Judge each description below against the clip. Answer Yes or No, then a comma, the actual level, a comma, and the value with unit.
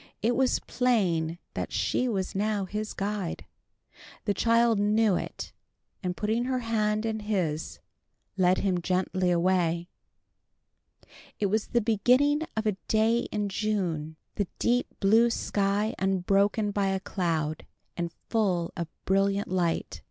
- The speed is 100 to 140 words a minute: Yes, slow, 135 wpm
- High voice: Yes, high, 200 Hz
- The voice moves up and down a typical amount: Yes, average, 3.2 semitones